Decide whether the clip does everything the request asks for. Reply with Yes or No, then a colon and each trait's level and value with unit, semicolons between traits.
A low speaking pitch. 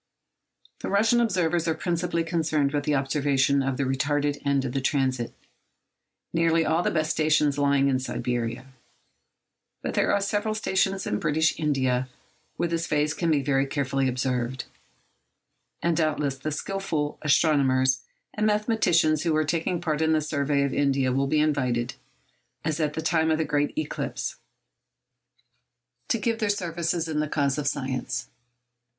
No: medium, 150 Hz